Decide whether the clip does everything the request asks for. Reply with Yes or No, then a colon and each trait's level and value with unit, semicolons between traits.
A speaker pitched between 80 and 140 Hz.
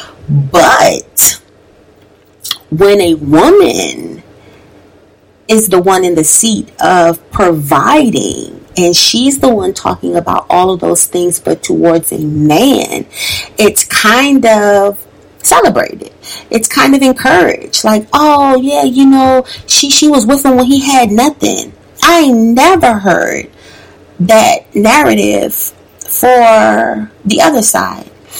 No: high, 230 Hz